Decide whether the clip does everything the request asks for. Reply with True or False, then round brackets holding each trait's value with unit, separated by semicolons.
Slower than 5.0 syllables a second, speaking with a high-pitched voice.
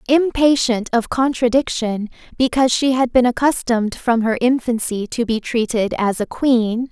True (4.7 syllables/s; 240 Hz)